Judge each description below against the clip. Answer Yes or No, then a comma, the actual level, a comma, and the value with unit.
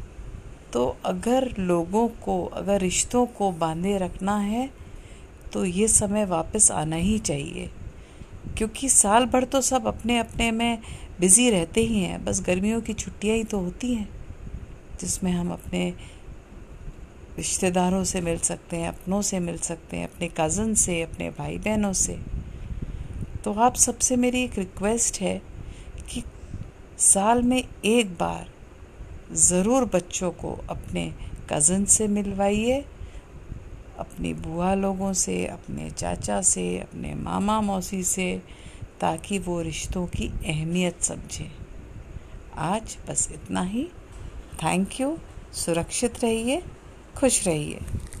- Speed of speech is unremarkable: Yes, average, 130 wpm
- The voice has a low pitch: No, medium, 185 Hz